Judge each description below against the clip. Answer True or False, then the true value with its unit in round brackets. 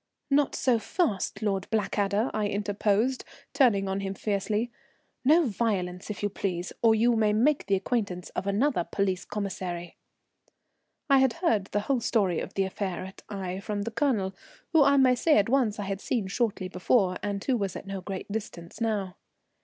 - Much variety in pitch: False (3.5 semitones)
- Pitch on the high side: True (205 Hz)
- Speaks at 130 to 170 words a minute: False (180 wpm)